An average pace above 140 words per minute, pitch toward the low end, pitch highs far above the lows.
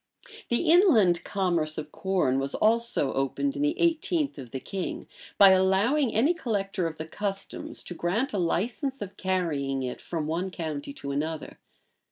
No: average, 165 wpm; high, 190 Hz; wide, 7.0 semitones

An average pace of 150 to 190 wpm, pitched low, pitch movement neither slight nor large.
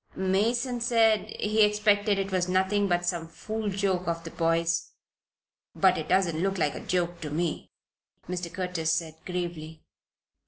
No: average, 155 wpm; medium, 185 Hz; average, 3.4 semitones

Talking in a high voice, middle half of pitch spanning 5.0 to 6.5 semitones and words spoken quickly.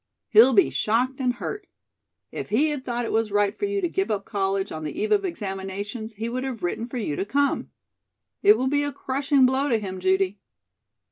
Yes: high, 235 Hz; wide, 5.6 semitones; fast, 215 wpm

